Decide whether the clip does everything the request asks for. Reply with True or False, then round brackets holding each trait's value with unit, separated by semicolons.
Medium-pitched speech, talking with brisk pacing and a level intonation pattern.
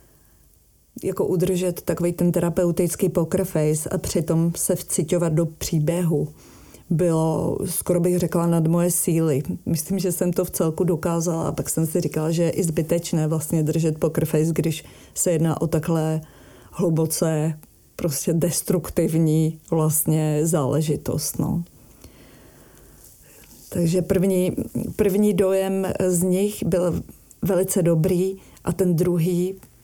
False (170 Hz; 125 wpm; 2.2 semitones)